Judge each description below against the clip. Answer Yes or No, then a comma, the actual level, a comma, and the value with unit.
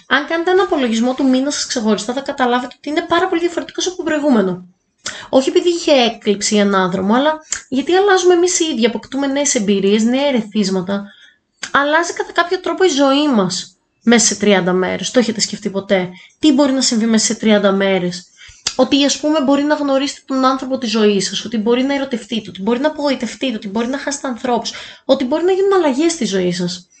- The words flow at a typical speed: No, fast, 200 wpm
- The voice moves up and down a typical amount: No, wide, 6.2 semitones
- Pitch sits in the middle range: No, very high, 260 Hz